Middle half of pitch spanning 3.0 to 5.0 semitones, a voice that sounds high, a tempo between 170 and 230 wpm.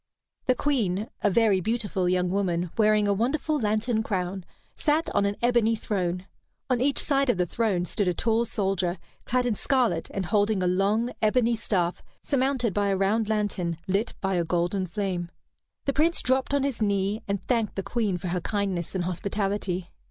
Yes: average, 4.0 semitones; high, 205 Hz; average, 180 wpm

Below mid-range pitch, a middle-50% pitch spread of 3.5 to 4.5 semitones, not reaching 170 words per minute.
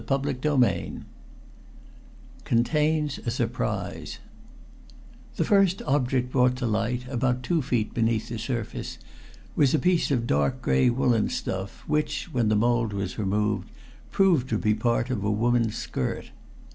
Yes: low, 120 Hz; average, 3.8 semitones; average, 140 wpm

